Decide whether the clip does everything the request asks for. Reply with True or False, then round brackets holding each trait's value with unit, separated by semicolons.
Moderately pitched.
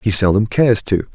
False (105 Hz)